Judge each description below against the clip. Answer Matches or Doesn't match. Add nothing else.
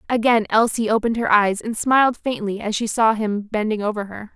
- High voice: Matches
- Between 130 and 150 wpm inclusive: Doesn't match